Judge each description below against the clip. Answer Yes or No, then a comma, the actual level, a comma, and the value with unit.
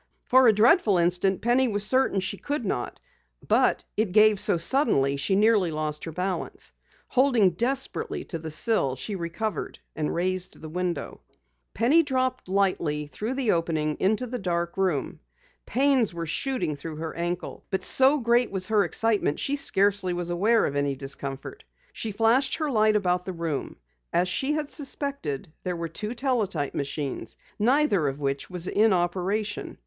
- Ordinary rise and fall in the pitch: No, wide, 5.8 semitones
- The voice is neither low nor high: No, high, 195 Hz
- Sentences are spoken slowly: No, average, 165 wpm